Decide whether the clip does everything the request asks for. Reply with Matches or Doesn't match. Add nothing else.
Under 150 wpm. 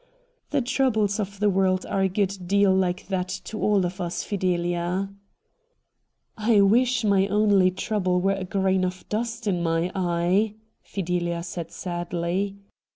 Doesn't match